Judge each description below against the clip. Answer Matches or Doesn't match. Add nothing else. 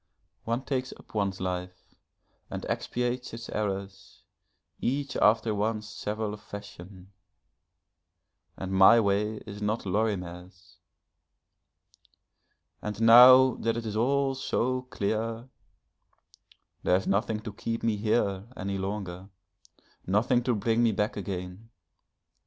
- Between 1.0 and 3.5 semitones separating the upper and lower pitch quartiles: Matches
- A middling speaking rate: Doesn't match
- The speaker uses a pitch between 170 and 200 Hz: Doesn't match